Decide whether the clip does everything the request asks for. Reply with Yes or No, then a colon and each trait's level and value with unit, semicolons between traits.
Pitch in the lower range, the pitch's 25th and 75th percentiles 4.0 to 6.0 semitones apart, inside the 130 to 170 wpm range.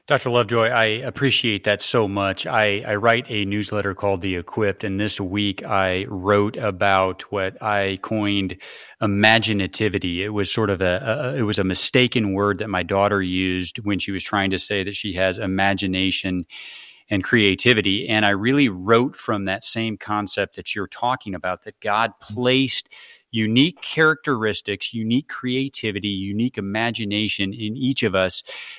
No: low, 105 Hz; average, 2.7 semitones; average, 160 wpm